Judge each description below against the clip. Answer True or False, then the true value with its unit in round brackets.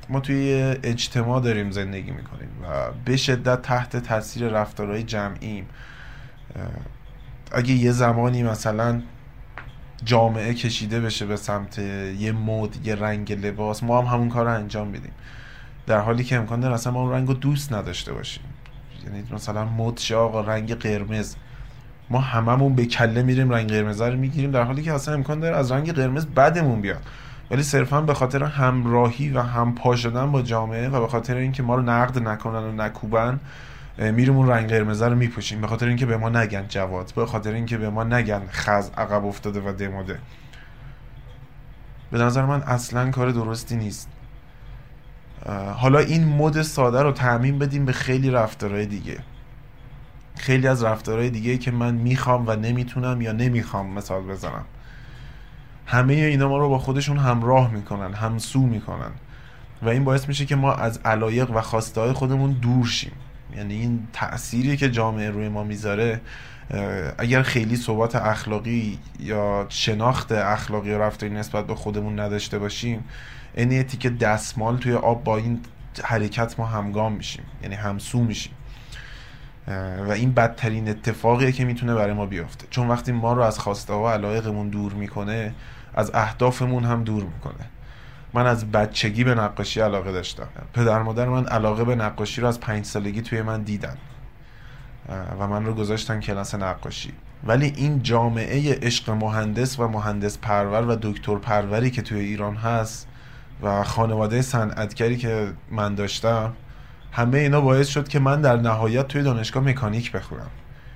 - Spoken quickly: True (160 wpm)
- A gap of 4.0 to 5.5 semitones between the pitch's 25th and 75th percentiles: False (3.2 semitones)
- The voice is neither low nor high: False (120 Hz)